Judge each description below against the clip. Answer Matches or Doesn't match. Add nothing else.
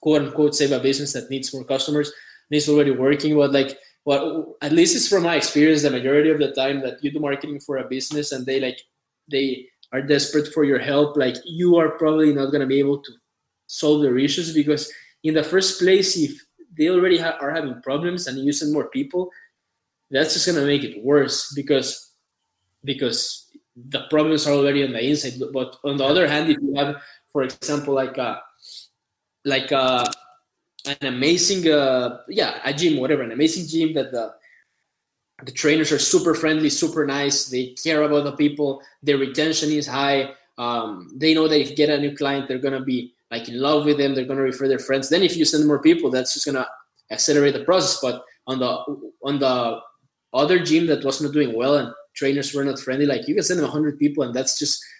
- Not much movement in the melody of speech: Matches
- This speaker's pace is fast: Matches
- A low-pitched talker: Doesn't match